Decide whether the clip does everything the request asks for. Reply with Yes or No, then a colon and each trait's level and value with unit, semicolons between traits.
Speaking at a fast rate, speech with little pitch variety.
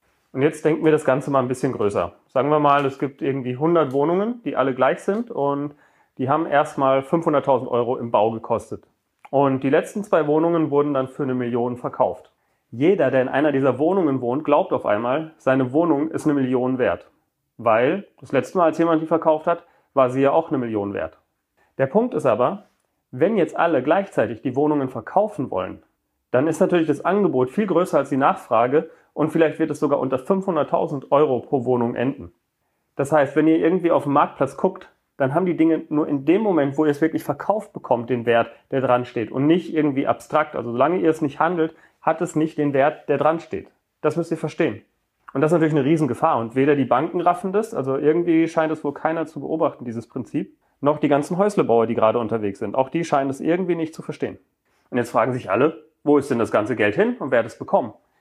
No: fast, 220 wpm; average, 3.6 semitones